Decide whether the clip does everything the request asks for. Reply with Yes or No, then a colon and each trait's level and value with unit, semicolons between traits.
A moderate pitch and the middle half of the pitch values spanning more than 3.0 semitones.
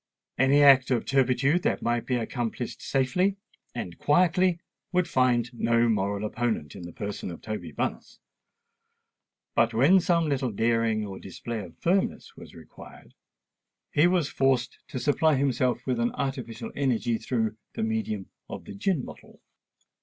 No: low, 125 Hz; average, 4.2 semitones